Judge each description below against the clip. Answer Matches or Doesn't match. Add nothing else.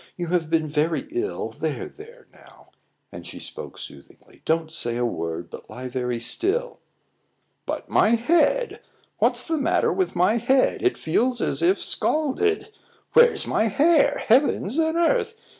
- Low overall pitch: Doesn't match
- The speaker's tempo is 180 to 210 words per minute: Doesn't match